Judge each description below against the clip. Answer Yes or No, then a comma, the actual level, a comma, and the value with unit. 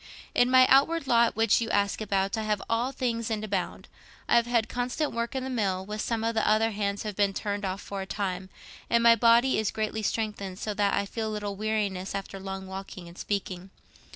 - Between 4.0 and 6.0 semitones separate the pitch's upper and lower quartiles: No, average, 2.8 semitones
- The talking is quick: Yes, fast, 220 wpm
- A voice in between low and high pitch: No, high, 215 Hz